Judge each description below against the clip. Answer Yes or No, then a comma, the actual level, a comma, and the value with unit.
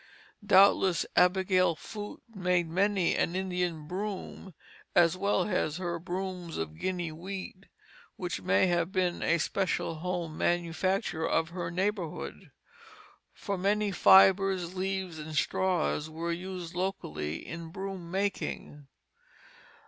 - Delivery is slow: Yes, slow, 120 wpm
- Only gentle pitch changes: Yes, narrow, 2.3 semitones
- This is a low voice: No, medium, 180 Hz